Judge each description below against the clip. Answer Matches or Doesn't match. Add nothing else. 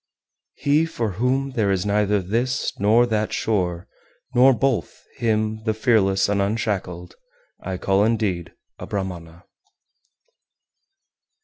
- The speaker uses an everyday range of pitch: Matches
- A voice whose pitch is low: Matches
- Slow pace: Matches